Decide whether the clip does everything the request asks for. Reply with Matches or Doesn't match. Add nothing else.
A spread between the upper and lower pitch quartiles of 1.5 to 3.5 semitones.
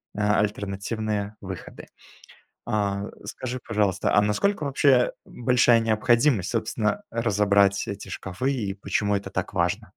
Matches